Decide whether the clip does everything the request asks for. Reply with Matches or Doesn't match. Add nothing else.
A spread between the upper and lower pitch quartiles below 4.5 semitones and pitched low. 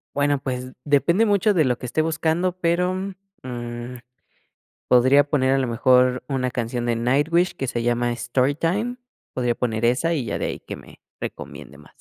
Doesn't match